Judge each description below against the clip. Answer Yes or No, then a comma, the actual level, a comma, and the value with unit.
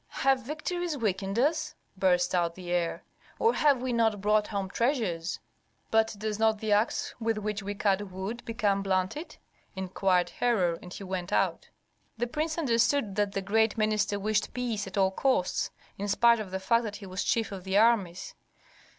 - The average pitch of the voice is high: Yes, high, 210 Hz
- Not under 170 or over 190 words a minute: Yes, average, 180 wpm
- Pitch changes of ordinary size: Yes, average, 3.6 semitones